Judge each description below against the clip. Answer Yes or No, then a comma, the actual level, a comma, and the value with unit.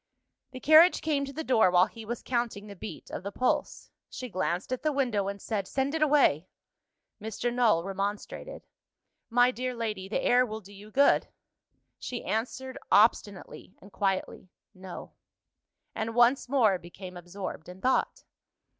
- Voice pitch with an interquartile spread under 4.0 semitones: No, average, 4.7 semitones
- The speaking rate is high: No, average, 160 wpm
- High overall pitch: Yes, high, 220 Hz